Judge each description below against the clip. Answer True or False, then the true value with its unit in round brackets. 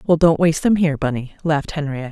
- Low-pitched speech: False (150 Hz)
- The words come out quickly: True (225 wpm)